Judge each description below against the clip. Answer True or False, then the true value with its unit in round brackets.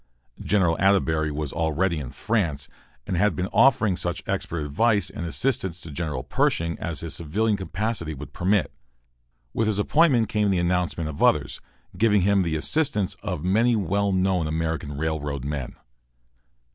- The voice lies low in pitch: True (90 Hz)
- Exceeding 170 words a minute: False (155 wpm)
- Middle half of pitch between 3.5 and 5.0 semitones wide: True (4.7 semitones)